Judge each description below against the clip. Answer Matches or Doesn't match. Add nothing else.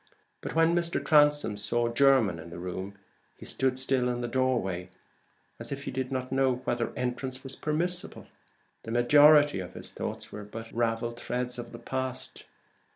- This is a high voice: Doesn't match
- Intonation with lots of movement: Doesn't match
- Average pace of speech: Matches